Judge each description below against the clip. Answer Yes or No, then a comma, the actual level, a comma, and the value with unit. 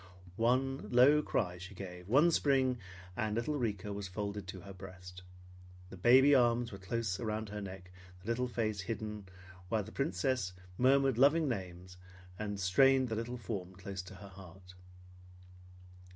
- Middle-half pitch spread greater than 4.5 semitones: Yes, average, 4.9 semitones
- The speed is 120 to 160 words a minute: Yes, average, 155 wpm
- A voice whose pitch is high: No, low, 105 Hz